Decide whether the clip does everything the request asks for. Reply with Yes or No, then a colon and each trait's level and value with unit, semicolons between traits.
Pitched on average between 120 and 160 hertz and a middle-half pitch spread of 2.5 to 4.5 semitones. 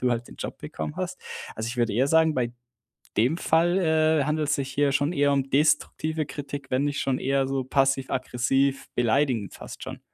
Yes: medium, 140 Hz; average, 2.8 semitones